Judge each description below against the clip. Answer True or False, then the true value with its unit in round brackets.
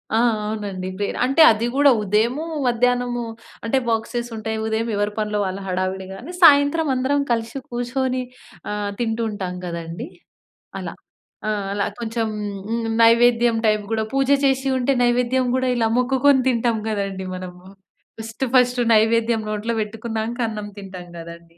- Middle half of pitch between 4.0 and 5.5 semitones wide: False (3.1 semitones)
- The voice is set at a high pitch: True (225 Hz)